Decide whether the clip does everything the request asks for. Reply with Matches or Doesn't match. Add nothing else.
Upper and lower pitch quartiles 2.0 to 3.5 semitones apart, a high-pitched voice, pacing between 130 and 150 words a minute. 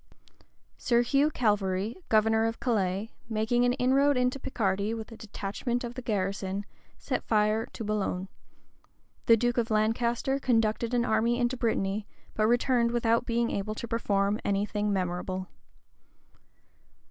Matches